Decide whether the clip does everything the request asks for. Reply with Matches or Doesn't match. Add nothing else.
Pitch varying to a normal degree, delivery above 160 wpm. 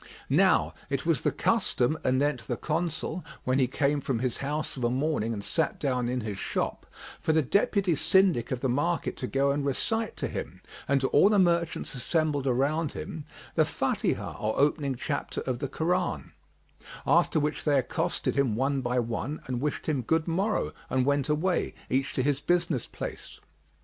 Matches